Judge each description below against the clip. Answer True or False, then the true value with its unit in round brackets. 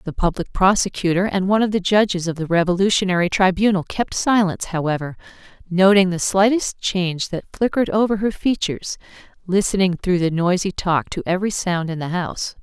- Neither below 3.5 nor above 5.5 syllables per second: False (5.9 syllables/s)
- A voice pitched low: False (185 Hz)